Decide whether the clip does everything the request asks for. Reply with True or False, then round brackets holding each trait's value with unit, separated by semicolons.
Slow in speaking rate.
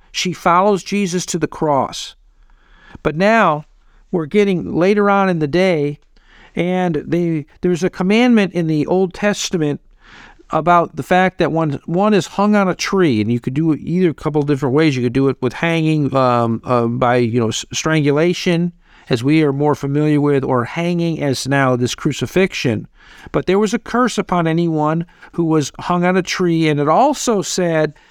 False (185 wpm)